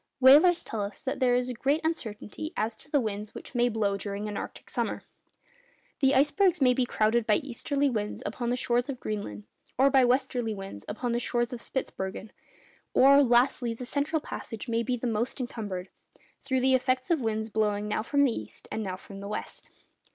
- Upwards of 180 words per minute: Yes, average, 195 wpm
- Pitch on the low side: No, high, 240 Hz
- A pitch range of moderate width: Yes, average, 3.7 semitones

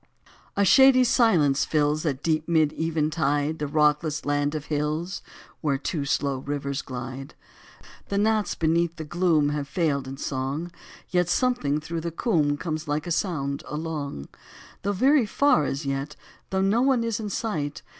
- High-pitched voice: No, medium, 155 Hz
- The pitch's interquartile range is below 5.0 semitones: Yes, average, 3.6 semitones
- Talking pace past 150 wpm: Yes, average, 160 wpm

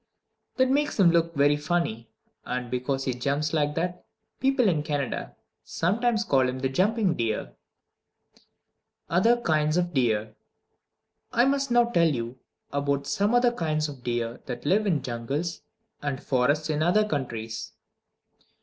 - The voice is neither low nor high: Yes, medium, 150 Hz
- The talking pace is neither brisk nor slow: Yes, average, 145 wpm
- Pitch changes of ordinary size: No, wide, 6.5 semitones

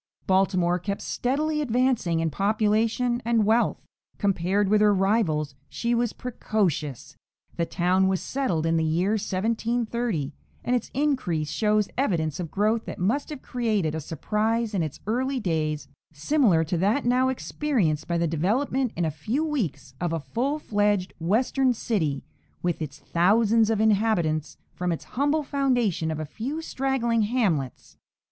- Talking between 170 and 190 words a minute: No, average, 155 wpm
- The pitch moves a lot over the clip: Yes, wide, 6.3 semitones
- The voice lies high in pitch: Yes, high, 210 Hz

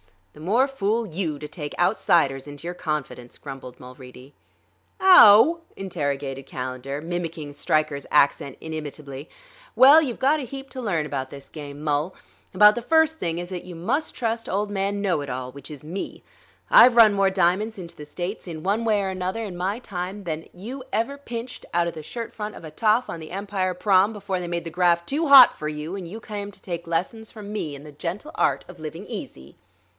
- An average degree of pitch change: No, wide, 5.9 semitones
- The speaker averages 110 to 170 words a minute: No, fast, 205 wpm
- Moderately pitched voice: Yes, medium, 180 Hz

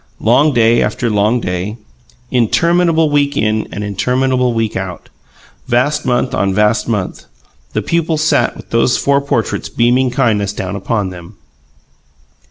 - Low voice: Yes, low, 120 Hz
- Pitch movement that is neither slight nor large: Yes, average, 4.4 semitones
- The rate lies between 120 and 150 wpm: Yes, average, 140 wpm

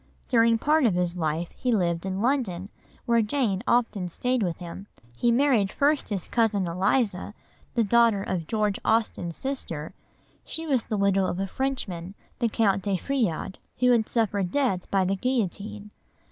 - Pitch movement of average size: Yes, average, 4.4 semitones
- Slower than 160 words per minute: No, average, 165 wpm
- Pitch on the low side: No, high, 205 Hz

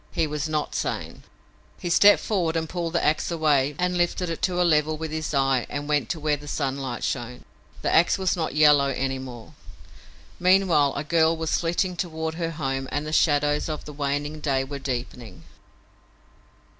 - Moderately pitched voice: Yes, medium, 150 Hz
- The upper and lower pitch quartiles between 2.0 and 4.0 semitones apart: Yes, average, 3.0 semitones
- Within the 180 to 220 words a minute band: Yes, average, 185 wpm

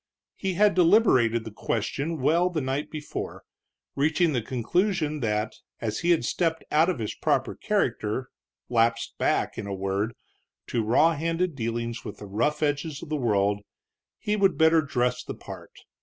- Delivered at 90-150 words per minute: No, average, 165 wpm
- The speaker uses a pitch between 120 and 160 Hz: Yes, medium, 140 Hz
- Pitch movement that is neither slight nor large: No, wide, 6.3 semitones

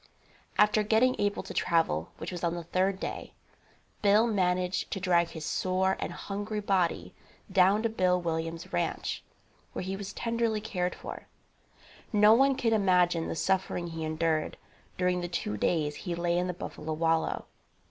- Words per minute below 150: No, average, 165 wpm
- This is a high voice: No, medium, 180 Hz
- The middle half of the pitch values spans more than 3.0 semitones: Yes, average, 3.4 semitones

